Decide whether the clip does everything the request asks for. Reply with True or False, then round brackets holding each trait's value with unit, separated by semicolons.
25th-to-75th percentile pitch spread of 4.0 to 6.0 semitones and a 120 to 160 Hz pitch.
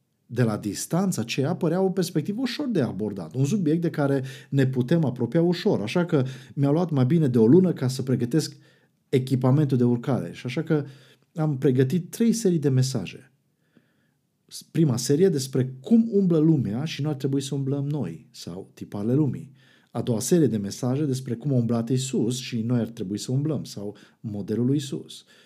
True (4.4 semitones; 140 Hz)